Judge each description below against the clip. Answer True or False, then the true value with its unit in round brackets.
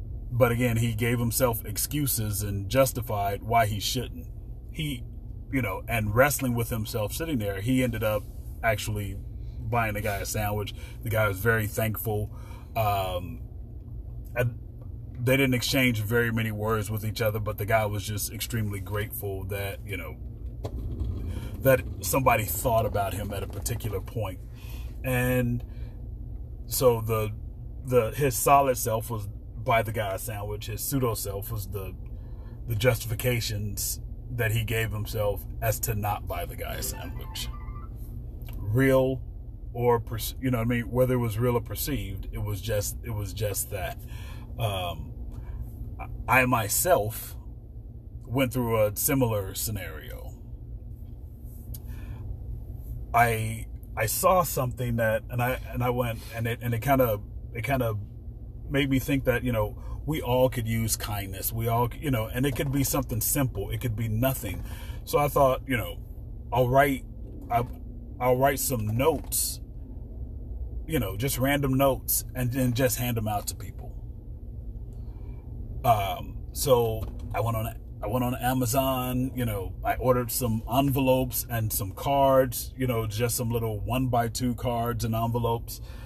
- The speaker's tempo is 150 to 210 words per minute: True (155 wpm)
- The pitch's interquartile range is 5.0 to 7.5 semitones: False (2.9 semitones)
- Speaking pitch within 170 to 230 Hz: False (115 Hz)